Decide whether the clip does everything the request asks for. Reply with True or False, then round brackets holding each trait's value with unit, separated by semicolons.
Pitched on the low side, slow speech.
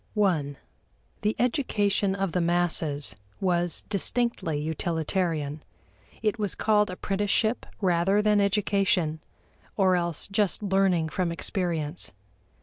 False (185 Hz; 105 wpm)